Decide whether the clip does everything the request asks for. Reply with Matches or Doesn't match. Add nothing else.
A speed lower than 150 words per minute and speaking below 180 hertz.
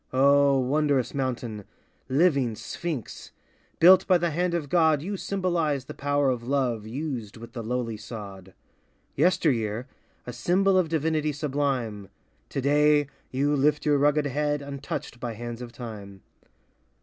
Matches